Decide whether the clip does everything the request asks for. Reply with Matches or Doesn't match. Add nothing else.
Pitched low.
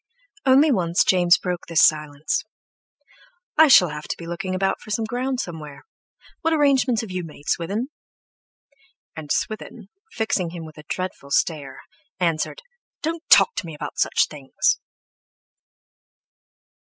Doesn't match